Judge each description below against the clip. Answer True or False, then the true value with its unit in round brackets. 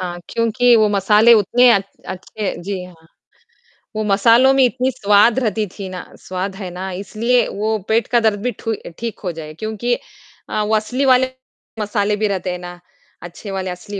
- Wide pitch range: False (3.3 semitones)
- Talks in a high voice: True (210 Hz)